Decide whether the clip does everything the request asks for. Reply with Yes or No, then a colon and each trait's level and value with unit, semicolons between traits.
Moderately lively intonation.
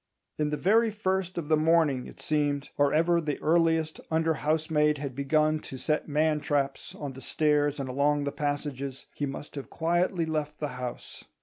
No: narrow, 2.1 semitones